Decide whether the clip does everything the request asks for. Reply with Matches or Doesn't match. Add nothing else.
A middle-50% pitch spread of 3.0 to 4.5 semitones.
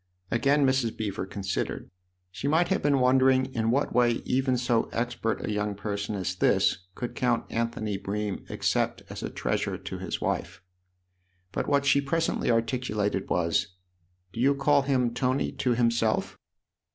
Matches